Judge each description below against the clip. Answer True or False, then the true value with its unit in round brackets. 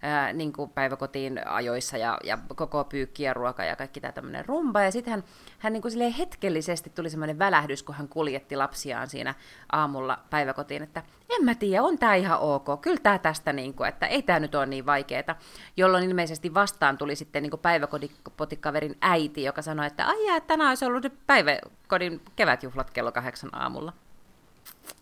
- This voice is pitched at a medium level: True (155 Hz)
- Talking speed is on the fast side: True (180 wpm)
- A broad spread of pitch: True (5.9 semitones)